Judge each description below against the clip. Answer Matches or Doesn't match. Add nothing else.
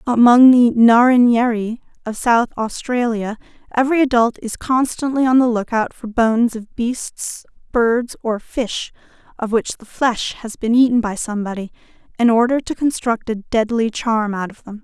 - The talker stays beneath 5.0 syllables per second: Matches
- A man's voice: Doesn't match